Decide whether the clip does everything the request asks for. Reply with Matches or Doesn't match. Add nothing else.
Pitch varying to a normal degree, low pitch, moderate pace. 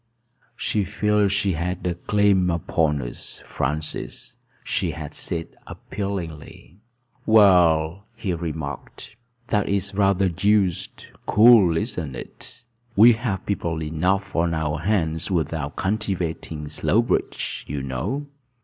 Doesn't match